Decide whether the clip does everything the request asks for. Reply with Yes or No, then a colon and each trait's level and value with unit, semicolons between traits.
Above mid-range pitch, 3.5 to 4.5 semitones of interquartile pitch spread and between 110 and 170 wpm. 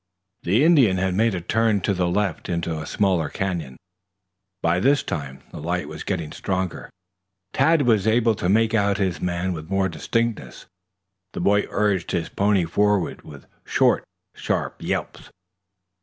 No: very low, 95 Hz; average, 3.8 semitones; average, 155 wpm